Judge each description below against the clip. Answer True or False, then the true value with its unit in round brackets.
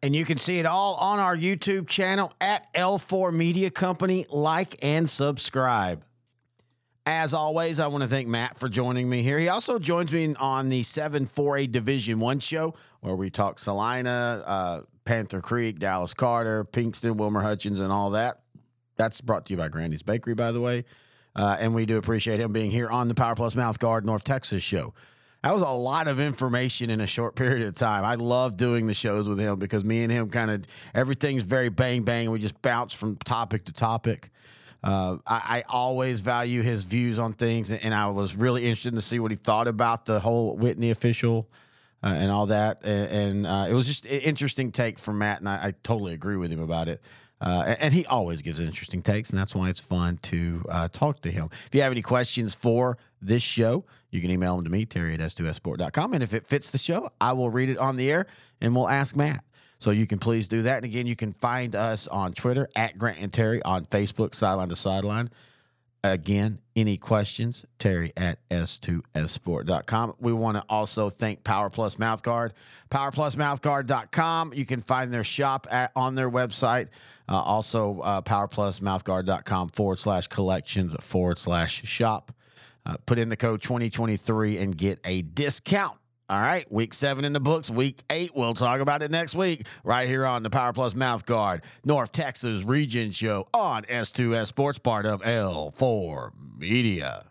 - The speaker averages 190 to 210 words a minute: True (195 wpm)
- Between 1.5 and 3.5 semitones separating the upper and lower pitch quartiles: False (4.0 semitones)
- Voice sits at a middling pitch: False (115 Hz)